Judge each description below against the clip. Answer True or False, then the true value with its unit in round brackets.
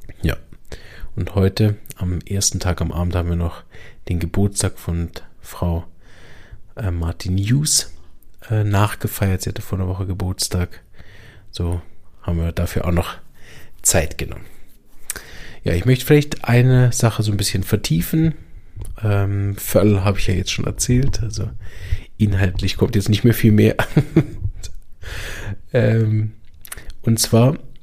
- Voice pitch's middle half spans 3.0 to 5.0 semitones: True (3.7 semitones)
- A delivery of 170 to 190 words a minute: False (135 wpm)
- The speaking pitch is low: True (100 Hz)